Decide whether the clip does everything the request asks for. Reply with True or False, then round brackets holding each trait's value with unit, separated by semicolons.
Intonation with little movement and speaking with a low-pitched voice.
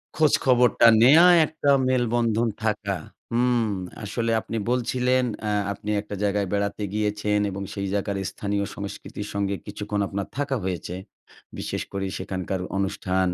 False (3.3 semitones; 105 Hz)